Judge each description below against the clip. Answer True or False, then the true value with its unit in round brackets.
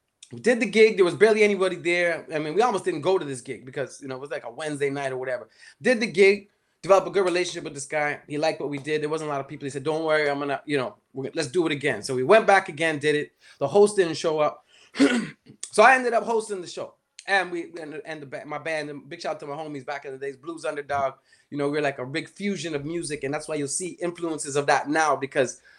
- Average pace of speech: False (290 wpm)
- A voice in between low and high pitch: True (155 Hz)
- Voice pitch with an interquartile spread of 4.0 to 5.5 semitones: True (4.7 semitones)